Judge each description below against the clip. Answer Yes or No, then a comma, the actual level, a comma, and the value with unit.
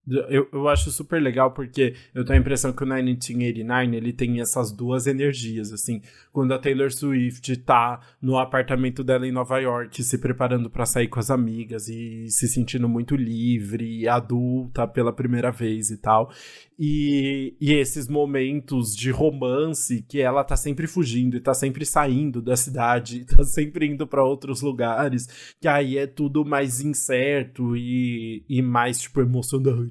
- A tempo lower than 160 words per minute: No, average, 165 wpm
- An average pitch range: No, narrow, 2.3 semitones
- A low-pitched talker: Yes, low, 130 Hz